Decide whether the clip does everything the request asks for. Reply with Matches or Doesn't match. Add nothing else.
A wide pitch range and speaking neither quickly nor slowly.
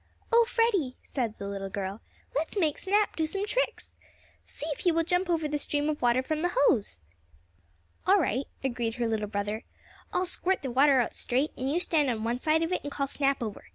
Doesn't match